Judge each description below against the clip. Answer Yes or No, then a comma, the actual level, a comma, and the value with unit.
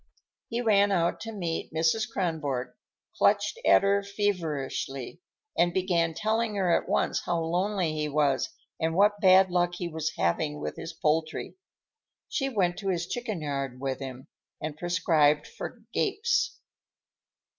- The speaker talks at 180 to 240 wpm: No, average, 145 wpm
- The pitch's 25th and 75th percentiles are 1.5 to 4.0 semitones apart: No, average, 4.6 semitones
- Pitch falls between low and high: Yes, medium, 175 Hz